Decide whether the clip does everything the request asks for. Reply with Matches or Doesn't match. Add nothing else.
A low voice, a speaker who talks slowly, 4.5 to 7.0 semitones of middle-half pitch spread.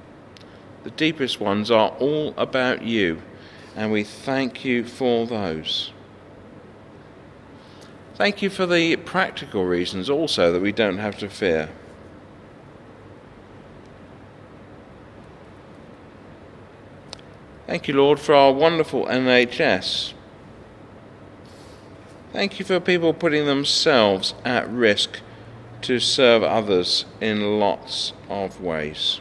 Matches